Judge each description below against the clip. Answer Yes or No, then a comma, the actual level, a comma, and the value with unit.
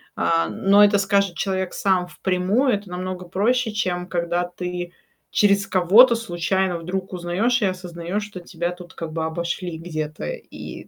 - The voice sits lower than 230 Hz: Yes, medium, 185 Hz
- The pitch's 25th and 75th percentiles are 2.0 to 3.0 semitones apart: Yes, narrow, 2.4 semitones